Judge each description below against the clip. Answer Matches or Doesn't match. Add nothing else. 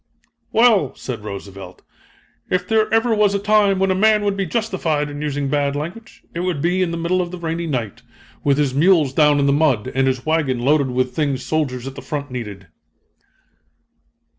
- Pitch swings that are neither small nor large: Doesn't match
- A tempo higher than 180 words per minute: Matches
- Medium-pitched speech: Matches